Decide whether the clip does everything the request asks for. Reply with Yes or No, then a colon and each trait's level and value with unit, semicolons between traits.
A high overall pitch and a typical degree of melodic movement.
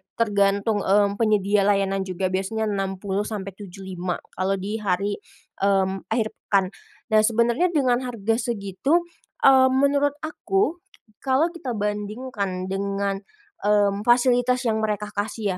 Yes: high, 205 Hz; average, 3.4 semitones